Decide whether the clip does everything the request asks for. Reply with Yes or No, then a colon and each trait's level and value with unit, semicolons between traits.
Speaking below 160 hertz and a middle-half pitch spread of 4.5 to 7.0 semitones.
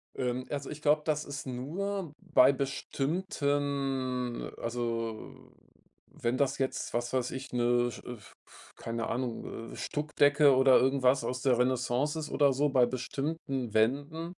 No: low, 135 Hz; average, 2.8 semitones